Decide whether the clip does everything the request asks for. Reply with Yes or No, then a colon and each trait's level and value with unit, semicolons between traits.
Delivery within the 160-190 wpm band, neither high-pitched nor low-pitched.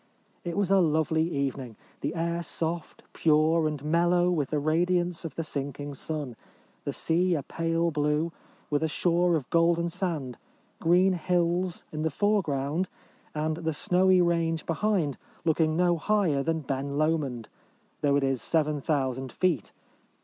No: average, 150 wpm; medium, 160 Hz